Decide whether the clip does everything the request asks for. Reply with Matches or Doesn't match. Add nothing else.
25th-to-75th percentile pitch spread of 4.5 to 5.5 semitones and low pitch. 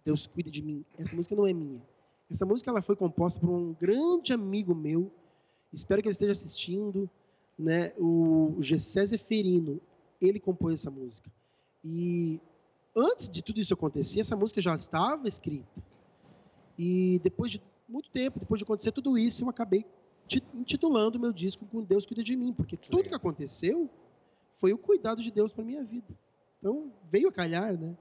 Doesn't match